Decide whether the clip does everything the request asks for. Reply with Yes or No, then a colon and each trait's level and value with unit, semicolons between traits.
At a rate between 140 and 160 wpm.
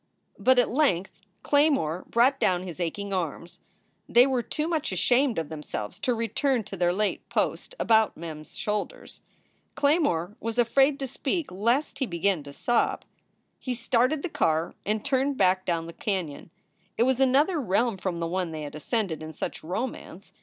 No: average, 175 wpm